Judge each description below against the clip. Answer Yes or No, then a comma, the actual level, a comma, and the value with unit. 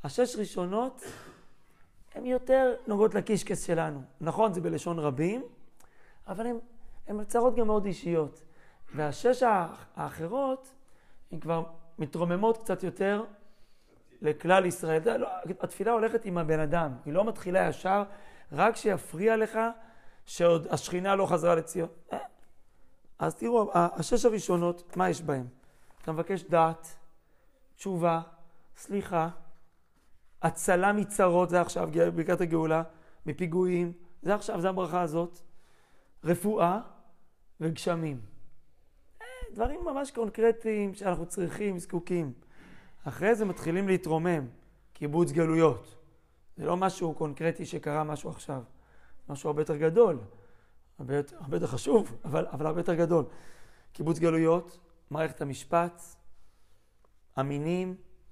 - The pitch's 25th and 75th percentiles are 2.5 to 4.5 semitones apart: Yes, average, 3.9 semitones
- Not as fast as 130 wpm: Yes, average, 110 wpm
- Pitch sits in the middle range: Yes, medium, 175 Hz